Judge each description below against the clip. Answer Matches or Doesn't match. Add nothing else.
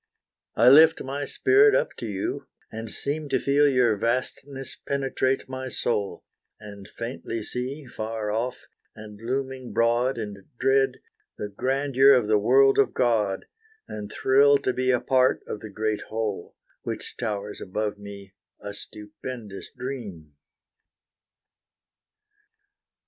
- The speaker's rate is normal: Doesn't match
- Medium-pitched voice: Doesn't match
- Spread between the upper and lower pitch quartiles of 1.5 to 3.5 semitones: Doesn't match